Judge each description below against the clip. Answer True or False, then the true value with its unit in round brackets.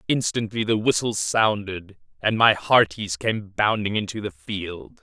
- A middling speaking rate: True (145 wpm)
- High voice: False (105 Hz)